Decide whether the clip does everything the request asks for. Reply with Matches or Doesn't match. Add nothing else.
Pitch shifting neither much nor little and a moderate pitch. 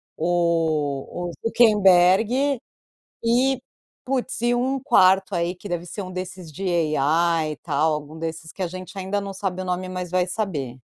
Matches